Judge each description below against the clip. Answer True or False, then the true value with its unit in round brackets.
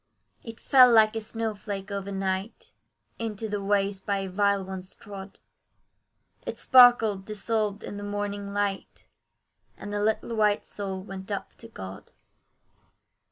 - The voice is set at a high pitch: True (205 Hz)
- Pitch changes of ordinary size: False (1.8 semitones)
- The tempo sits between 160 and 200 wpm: False (140 wpm)